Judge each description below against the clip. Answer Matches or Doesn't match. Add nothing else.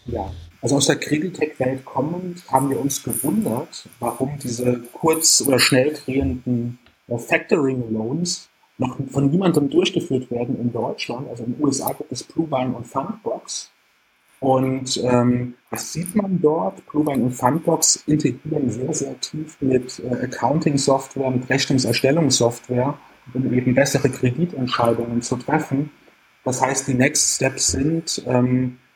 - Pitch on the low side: Matches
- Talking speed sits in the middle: Matches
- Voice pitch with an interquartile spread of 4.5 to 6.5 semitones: Doesn't match